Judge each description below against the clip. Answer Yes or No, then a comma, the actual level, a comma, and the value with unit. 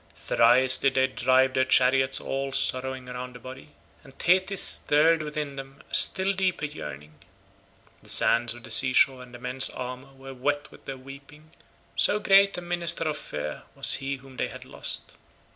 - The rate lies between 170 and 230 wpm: Yes, average, 180 wpm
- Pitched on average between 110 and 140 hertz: Yes, low, 135 Hz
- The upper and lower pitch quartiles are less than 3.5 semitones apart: Yes, average, 2.9 semitones